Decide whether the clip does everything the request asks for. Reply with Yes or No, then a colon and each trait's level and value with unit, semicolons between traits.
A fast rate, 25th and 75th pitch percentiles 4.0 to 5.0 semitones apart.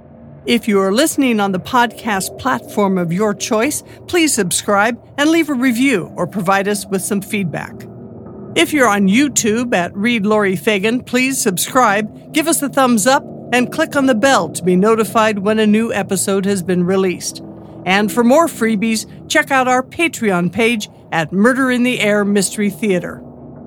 No: average, 175 wpm; average, 4.4 semitones